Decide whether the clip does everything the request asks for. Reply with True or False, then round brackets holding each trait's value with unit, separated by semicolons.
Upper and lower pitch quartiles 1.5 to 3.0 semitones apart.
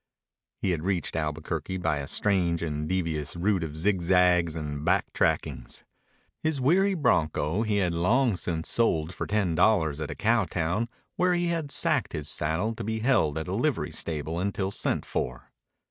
False (5.3 semitones)